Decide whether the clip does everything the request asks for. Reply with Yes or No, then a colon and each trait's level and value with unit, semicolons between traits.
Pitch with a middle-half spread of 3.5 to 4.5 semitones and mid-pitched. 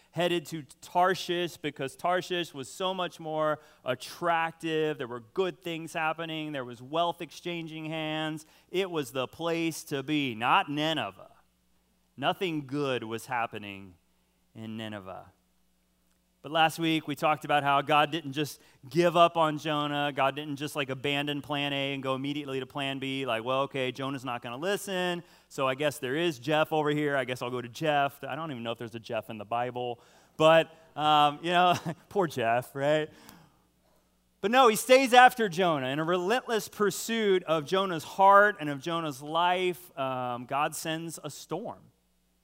Yes: average, 4.2 semitones; medium, 150 Hz